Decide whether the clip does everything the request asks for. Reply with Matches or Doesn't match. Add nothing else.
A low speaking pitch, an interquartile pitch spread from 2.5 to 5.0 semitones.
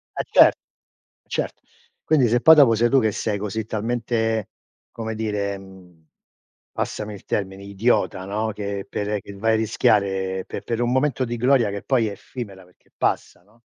Matches